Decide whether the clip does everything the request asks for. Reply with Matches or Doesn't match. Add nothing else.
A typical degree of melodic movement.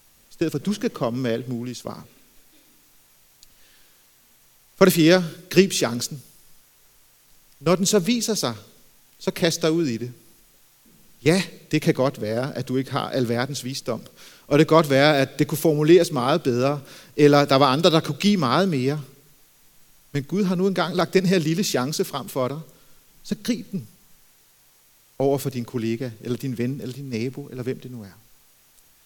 Matches